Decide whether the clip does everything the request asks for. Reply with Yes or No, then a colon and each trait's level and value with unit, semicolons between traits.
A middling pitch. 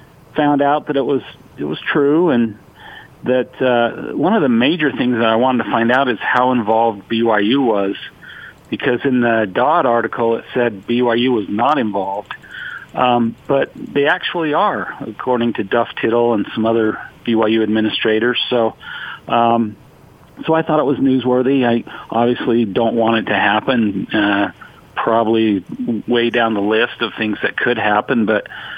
No: low, 115 Hz